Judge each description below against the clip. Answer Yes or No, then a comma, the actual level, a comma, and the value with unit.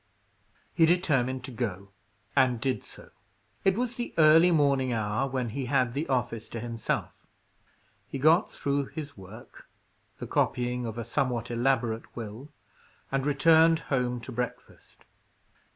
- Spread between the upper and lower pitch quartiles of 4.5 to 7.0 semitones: No, average, 3.8 semitones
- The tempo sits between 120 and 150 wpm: Yes, average, 140 wpm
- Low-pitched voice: Yes, low, 130 Hz